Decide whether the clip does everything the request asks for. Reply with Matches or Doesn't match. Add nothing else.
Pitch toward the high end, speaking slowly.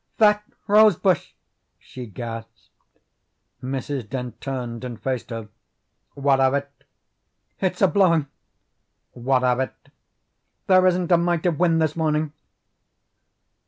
Doesn't match